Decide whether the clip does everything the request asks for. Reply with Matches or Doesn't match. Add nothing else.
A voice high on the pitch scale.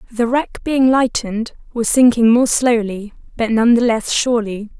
Matches